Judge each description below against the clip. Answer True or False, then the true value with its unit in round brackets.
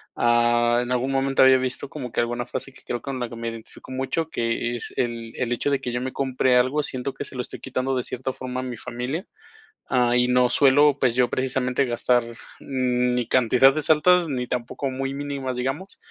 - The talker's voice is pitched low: True (125 Hz)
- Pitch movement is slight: True (1.7 semitones)